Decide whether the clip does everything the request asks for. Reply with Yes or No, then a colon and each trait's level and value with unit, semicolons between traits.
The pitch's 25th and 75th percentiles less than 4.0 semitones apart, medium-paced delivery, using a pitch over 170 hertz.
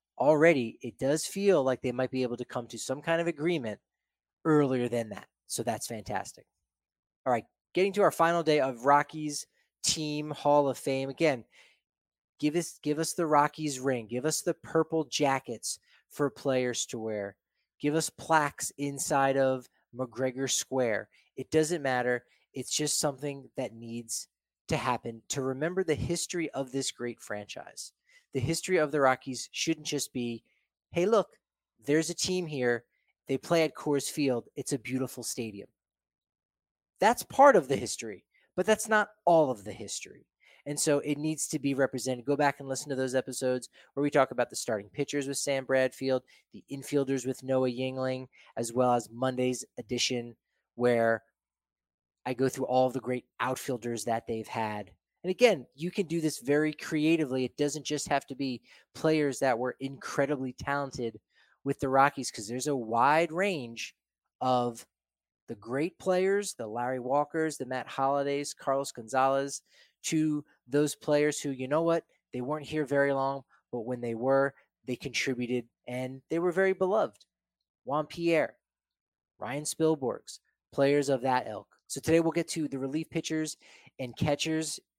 No: average, 3.5 semitones; average, 165 wpm; low, 135 Hz